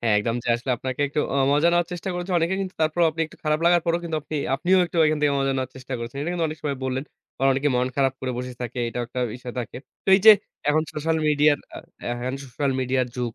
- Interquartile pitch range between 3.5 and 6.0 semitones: Yes, average, 4.2 semitones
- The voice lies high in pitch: No, medium, 140 Hz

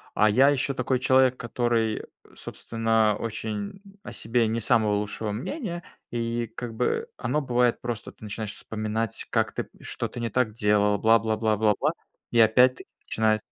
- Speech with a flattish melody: Yes, narrow, 2.3 semitones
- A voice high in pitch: No, low, 115 Hz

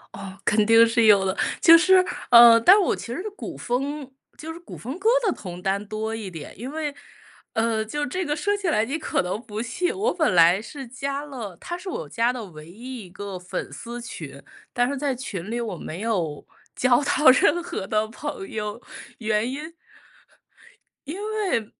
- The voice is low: No, high, 235 Hz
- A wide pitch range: Yes, wide, 5.9 semitones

